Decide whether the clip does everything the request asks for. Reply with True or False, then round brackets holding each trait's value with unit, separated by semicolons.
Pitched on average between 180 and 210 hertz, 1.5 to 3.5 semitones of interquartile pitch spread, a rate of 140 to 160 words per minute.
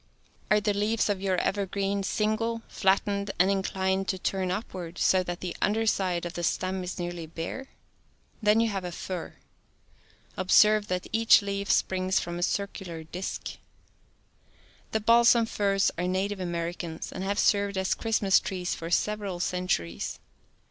True (190 Hz; 2.4 semitones; 155 wpm)